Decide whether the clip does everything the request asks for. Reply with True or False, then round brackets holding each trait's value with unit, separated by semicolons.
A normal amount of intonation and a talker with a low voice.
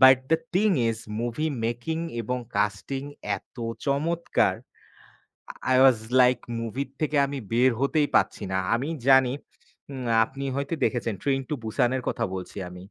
True (3.1 semitones; 130 Hz)